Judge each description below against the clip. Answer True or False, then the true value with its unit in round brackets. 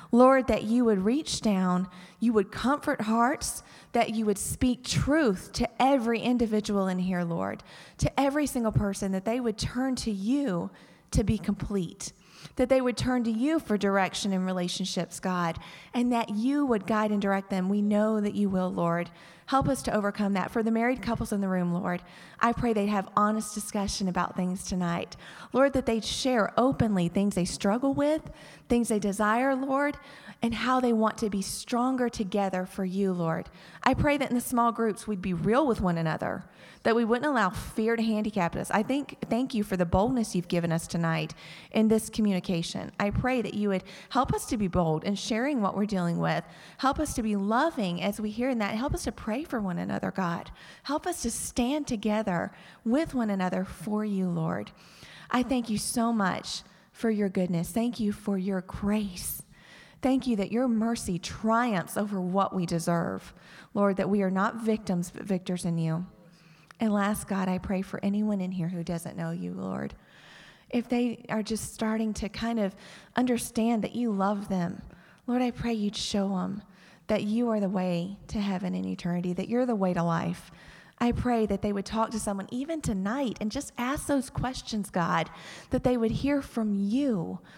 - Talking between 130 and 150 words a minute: False (195 wpm)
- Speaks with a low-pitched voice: False (210 Hz)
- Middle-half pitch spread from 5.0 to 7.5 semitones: False (4.1 semitones)